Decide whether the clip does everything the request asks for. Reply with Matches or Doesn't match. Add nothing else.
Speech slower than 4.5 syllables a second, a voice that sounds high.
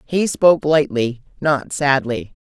Doesn't match